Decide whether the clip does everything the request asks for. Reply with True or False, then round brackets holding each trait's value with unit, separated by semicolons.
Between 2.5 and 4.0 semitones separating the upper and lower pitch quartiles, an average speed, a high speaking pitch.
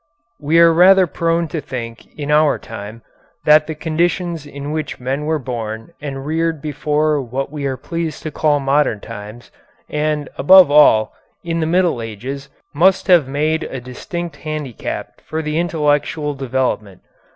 False (3.3 semitones; 155 wpm; 150 Hz)